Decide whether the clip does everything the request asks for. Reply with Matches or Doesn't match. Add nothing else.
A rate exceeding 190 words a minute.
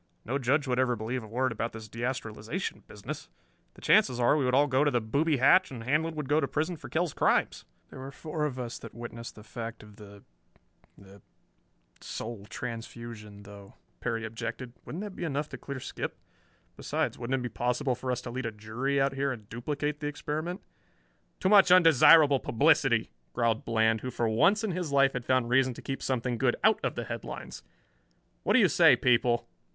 Matches